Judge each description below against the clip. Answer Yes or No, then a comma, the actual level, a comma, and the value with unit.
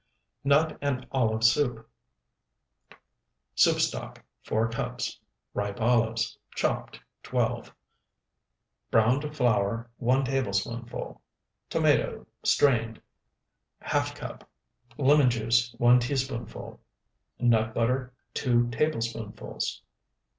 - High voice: No, low, 120 Hz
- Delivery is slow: Yes, slow, 80 wpm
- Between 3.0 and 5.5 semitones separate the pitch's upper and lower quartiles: No, narrow, 2.6 semitones